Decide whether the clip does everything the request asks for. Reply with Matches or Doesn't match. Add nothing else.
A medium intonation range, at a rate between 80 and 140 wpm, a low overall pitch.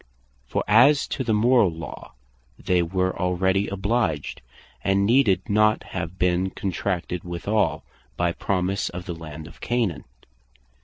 Matches